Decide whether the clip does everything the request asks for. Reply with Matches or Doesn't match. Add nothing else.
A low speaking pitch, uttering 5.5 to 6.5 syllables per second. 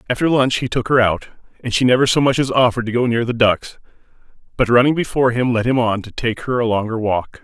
Matches